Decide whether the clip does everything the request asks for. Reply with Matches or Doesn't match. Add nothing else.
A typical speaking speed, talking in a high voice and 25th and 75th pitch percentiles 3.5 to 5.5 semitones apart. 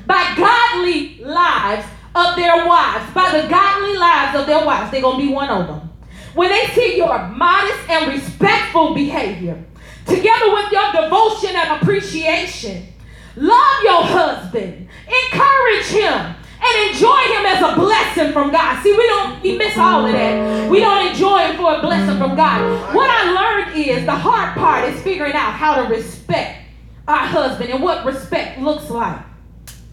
Matches